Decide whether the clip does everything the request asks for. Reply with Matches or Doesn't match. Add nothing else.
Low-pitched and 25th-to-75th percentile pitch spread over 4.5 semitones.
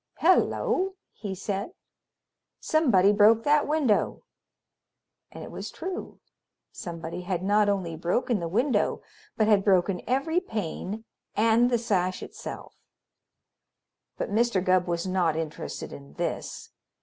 Doesn't match